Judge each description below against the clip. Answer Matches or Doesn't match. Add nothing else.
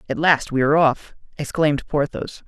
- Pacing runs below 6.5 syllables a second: Matches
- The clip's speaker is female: Doesn't match